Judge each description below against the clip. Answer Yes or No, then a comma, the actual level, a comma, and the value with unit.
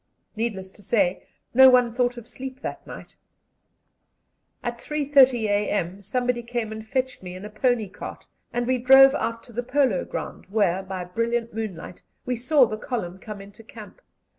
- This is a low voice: No, high, 230 Hz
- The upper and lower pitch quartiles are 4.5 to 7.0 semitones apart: No, average, 3.6 semitones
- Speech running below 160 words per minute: No, average, 170 wpm